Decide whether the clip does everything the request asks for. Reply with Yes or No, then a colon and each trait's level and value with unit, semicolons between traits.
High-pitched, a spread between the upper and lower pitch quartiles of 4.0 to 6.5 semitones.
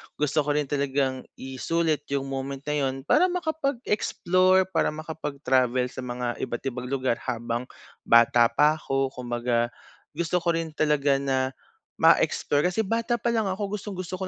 No: medium, 145 Hz; wide, 5.5 semitones